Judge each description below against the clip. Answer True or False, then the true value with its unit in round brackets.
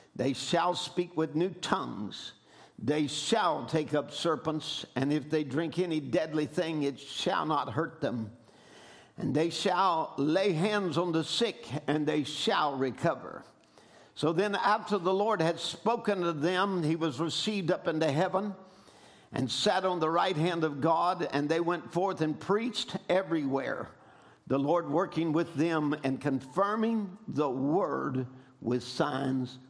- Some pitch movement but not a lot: True (3.8 semitones)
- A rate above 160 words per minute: False (155 wpm)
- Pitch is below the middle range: False (160 Hz)